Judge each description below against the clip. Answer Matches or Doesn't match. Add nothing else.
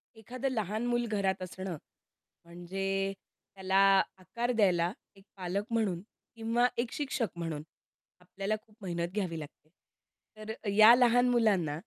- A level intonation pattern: Doesn't match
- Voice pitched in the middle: Doesn't match